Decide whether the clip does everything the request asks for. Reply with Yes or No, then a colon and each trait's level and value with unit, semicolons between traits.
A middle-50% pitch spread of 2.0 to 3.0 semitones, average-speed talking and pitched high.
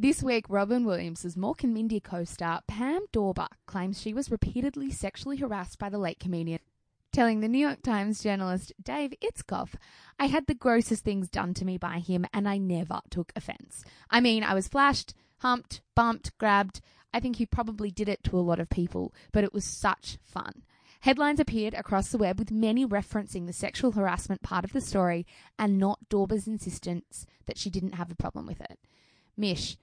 No: average, 4.3 semitones; average, 190 wpm; high, 205 Hz